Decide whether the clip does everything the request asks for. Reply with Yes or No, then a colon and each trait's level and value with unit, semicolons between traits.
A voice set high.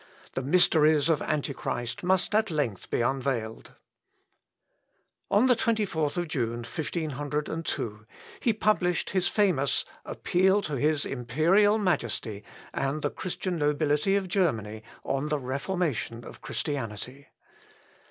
No: medium, 150 Hz